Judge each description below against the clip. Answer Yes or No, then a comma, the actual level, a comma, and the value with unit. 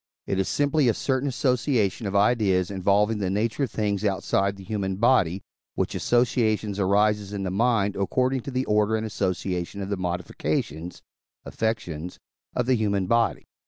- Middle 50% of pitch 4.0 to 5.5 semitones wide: No, average, 3.3 semitones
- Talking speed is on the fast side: No, average, 160 wpm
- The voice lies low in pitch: Yes, low, 105 Hz